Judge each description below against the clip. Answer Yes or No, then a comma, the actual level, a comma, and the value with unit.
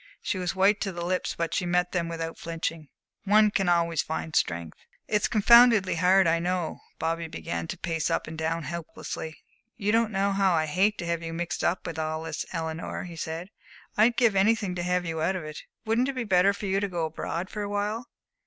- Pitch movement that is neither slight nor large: Yes, average, 3.4 semitones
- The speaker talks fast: Yes, fast, 220 wpm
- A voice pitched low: No, medium, 175 Hz